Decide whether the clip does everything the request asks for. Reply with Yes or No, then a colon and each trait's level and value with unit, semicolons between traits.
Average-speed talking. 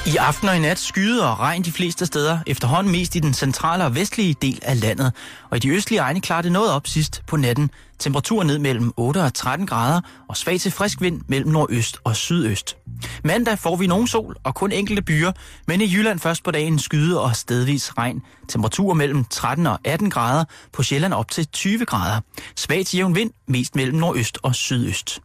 Yes: average, 210 wpm